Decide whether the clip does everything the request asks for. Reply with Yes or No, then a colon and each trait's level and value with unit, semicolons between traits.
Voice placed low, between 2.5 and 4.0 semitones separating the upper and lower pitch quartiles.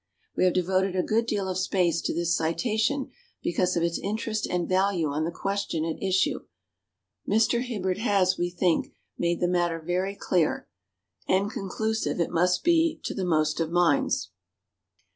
No: medium, 185 Hz; average, 2.9 semitones